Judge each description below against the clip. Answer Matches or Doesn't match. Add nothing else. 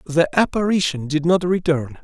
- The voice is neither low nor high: Matches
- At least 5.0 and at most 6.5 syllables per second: Doesn't match